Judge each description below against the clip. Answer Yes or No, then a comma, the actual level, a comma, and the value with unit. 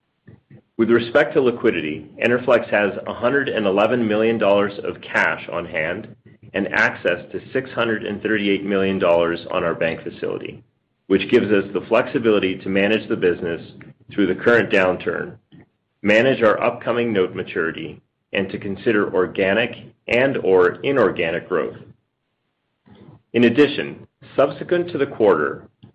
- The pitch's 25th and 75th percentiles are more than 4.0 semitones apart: Yes, average, 5.1 semitones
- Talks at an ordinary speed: No, slow, 125 wpm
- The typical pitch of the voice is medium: No, low, 110 Hz